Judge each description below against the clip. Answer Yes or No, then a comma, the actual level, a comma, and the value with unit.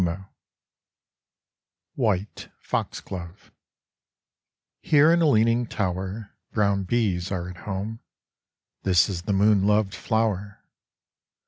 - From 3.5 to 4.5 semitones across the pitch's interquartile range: No, average, 2.9 semitones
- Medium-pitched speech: No, low, 100 Hz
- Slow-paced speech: Yes, slow, 100 wpm